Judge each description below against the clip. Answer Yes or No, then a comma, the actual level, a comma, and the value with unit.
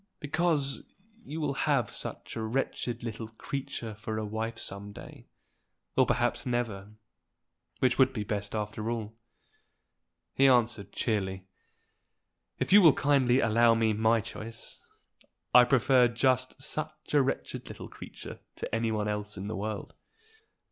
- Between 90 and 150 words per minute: Yes, average, 140 wpm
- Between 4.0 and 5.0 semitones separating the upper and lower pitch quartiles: No, average, 3.5 semitones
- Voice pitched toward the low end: Yes, low, 115 Hz